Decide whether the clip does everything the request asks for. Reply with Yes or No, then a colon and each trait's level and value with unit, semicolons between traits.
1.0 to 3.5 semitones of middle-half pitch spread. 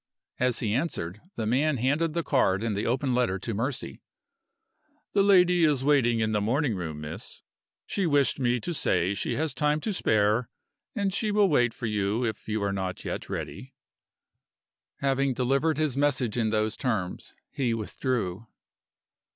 No: average, 5.3 semitones